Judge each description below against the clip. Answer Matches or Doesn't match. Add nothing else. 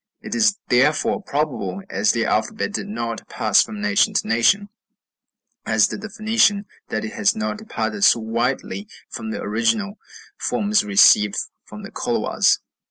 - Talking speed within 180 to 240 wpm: Doesn't match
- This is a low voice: Doesn't match